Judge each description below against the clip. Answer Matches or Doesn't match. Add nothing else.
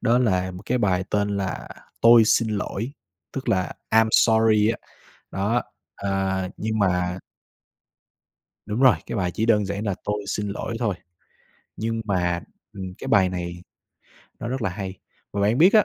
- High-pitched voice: Doesn't match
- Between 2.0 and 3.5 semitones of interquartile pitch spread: Matches